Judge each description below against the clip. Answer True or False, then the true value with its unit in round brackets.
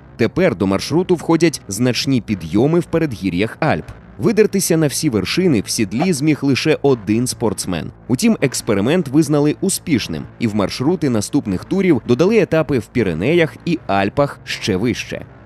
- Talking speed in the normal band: True (140 wpm)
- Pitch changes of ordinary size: False (6.9 semitones)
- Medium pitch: True (145 Hz)